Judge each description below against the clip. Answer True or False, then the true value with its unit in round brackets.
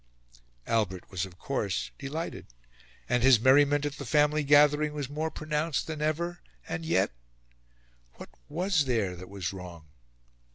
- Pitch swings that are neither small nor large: False (7.2 semitones)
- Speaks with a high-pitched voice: False (145 Hz)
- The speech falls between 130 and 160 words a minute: True (140 wpm)